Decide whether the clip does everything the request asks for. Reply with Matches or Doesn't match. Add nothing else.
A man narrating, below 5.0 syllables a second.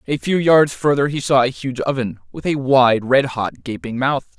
Matches